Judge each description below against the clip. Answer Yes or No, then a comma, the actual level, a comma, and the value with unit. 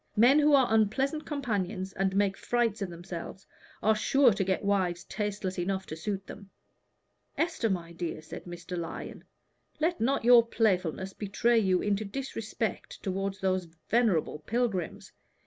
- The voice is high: Yes, high, 200 Hz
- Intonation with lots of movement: No, average, 3.9 semitones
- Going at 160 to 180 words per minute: No, average, 145 wpm